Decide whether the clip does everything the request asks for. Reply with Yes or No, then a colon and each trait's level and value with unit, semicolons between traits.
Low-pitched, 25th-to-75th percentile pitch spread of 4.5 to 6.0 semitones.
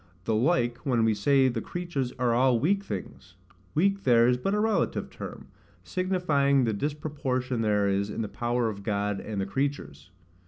Yes: low, 125 Hz; average, 5.0 semitones